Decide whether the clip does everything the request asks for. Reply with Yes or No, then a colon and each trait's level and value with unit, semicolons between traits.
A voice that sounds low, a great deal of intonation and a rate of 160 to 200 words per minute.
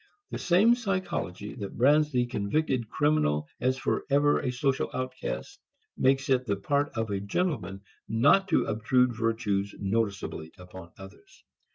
No: low, 125 Hz; wide, 6.2 semitones; average, 140 wpm